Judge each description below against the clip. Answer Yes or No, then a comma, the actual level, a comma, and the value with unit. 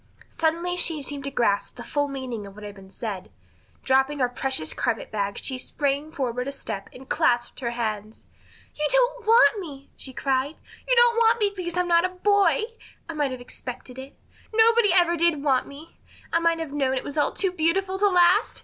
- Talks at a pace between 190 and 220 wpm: Yes, fast, 205 wpm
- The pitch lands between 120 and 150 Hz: No, very high, 290 Hz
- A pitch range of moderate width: No, wide, 6.0 semitones